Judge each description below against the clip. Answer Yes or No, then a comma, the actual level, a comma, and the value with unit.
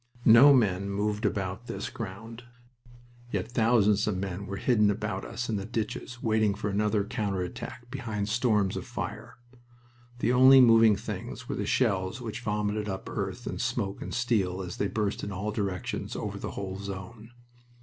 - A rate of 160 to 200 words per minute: Yes, average, 170 wpm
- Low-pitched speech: Yes, low, 105 Hz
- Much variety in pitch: No, average, 2.8 semitones